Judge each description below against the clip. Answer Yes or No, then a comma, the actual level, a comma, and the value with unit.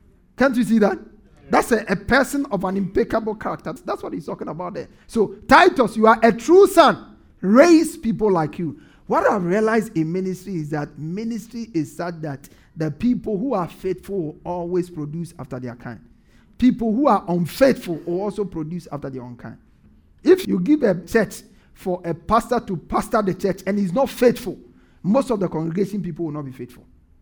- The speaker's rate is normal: Yes, average, 190 wpm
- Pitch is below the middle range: No, high, 195 Hz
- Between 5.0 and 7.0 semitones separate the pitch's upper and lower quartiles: Yes, wide, 5.5 semitones